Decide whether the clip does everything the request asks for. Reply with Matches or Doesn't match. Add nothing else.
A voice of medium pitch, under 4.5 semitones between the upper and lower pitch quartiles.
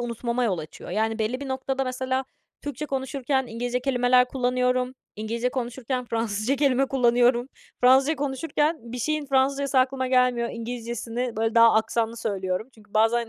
Doesn't match